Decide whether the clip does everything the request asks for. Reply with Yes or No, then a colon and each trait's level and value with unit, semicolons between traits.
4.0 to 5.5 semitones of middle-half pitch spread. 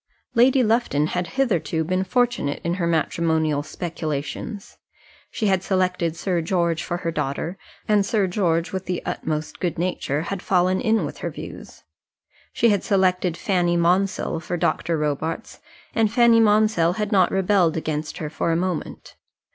No: average, 3.5 semitones